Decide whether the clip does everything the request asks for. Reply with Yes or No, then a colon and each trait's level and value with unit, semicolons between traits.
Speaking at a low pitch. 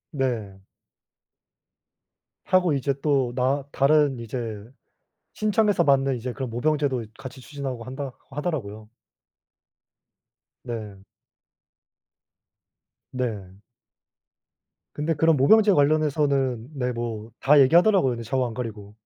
Yes: low, 130 Hz